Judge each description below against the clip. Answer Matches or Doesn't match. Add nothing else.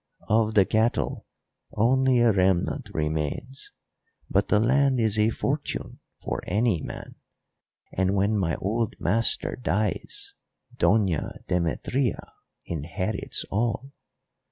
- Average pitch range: Matches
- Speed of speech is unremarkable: Doesn't match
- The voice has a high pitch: Doesn't match